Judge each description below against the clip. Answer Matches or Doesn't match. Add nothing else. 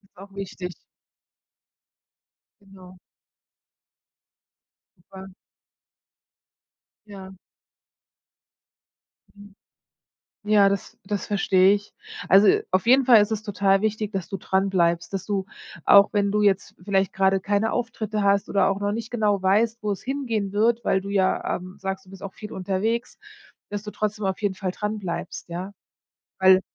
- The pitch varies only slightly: Matches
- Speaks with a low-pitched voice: Doesn't match